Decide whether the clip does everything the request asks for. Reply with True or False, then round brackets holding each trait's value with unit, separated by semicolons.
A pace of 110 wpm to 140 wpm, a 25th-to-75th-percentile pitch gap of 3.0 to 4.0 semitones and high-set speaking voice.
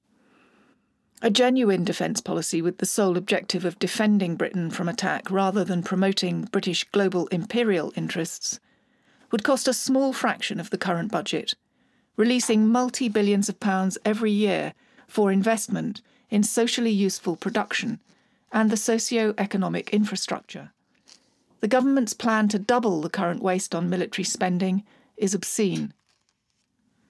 True (135 wpm; 3.6 semitones; 210 Hz)